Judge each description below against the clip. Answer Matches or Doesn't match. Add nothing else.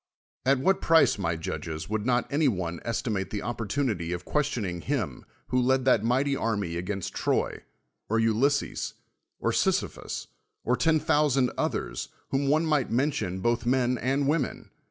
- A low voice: Matches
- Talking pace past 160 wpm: Doesn't match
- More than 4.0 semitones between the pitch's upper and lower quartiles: Matches